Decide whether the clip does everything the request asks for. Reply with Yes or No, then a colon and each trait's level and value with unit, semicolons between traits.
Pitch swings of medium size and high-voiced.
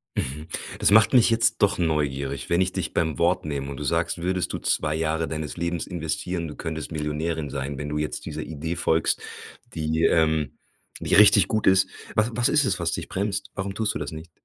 No: average, 3.6 semitones; very low, 80 Hz